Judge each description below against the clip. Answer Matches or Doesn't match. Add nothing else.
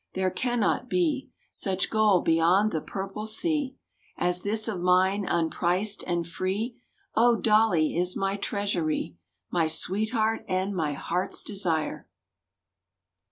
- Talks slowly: Matches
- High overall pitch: Matches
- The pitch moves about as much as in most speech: Matches